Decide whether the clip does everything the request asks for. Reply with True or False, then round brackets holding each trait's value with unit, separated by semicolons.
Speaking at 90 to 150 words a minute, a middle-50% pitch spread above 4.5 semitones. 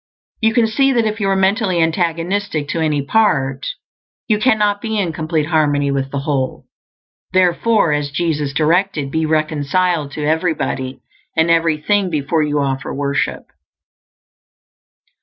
True (140 wpm; 5.0 semitones)